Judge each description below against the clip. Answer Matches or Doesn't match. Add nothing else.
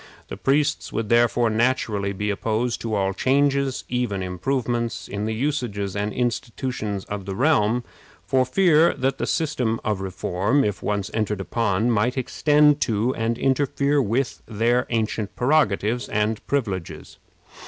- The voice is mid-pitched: Doesn't match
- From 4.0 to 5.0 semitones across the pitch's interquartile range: Matches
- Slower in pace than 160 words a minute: Matches